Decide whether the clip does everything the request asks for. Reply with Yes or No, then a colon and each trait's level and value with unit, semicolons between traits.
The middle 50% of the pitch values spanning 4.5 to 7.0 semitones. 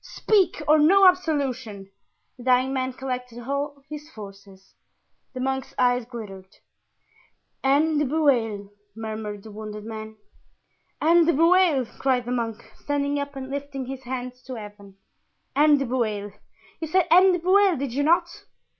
Yes: average, 4.9 semitones